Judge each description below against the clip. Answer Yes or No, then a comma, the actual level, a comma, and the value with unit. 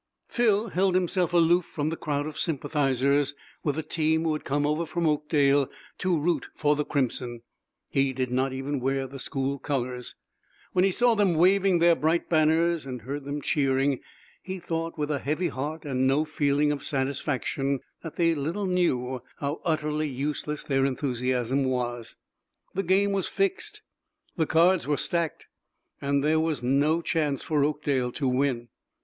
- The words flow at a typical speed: Yes, average, 165 wpm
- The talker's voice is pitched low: No, medium, 150 Hz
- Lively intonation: No, average, 3.5 semitones